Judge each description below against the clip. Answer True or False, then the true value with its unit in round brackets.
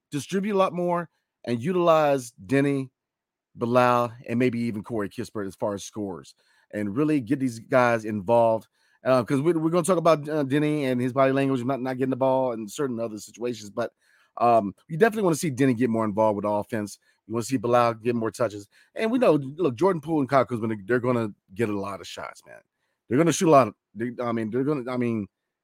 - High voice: False (125 Hz)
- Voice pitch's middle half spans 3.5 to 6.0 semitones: True (4.2 semitones)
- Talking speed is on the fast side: True (230 wpm)